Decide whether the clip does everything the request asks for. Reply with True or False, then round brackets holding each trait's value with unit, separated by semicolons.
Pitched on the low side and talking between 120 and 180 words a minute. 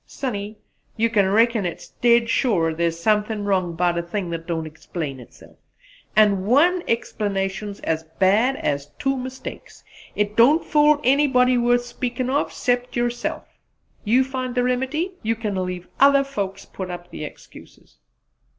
False (220 Hz; 150 wpm)